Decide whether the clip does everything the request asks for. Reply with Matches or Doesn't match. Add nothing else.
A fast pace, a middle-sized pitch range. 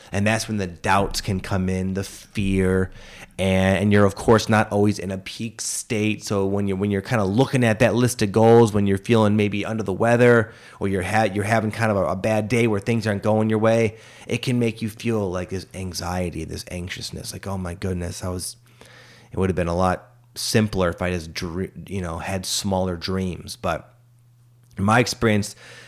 Matches